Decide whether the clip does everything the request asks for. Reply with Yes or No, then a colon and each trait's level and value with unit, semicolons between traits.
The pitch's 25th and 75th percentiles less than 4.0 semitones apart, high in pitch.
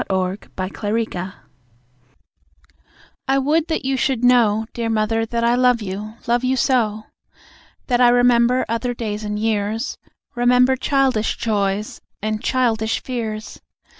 Yes: average, 2.7 semitones; high, 230 Hz